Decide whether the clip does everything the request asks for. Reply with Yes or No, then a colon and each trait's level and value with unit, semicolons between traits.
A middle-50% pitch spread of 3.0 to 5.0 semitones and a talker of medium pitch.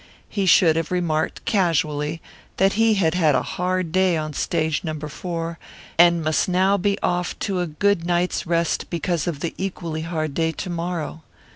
No: narrow, 2.5 semitones; medium, 170 Hz